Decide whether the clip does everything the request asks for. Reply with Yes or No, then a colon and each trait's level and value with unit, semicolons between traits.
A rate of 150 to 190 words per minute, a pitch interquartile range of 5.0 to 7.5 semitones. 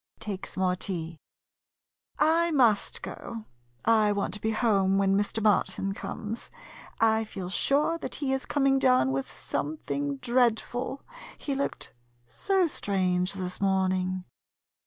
No: slow, 135 wpm; average, 5.3 semitones